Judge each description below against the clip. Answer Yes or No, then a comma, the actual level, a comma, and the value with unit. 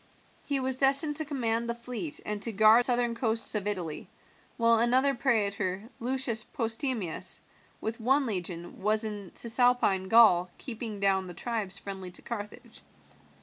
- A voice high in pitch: Yes, high, 225 Hz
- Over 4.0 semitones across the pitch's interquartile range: No, average, 3.7 semitones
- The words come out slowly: No, average, 150 wpm